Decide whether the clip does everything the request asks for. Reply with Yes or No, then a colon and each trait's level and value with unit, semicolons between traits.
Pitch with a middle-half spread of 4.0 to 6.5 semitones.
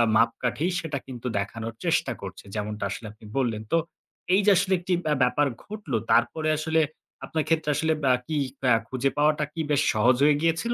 Yes: average, 5.3 semitones